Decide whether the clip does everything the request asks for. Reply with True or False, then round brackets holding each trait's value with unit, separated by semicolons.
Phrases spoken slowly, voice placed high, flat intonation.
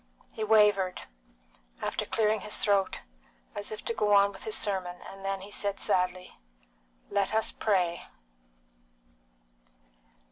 True (130 wpm; 200 Hz; 1.8 semitones)